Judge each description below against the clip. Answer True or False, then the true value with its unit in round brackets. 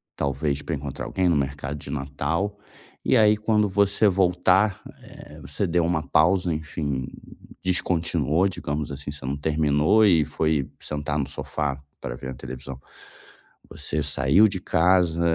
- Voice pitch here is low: True (80 Hz)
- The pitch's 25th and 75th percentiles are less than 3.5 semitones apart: False (4.4 semitones)